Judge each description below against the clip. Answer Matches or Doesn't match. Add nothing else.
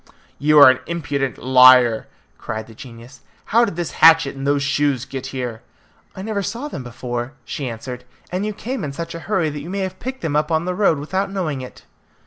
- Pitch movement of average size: Doesn't match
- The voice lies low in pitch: Doesn't match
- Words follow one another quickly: Matches